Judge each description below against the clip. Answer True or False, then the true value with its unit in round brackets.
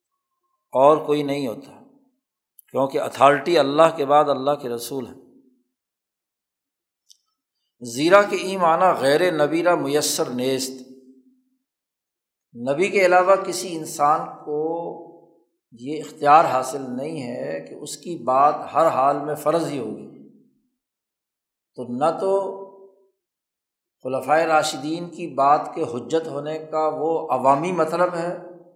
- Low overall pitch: False (165 Hz)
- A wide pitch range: False (5.0 semitones)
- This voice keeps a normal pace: True (120 wpm)